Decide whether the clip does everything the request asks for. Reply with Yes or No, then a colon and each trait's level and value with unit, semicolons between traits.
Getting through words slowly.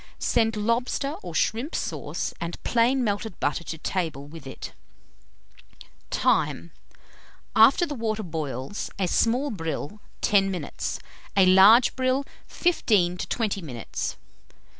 Yes: slow, 120 wpm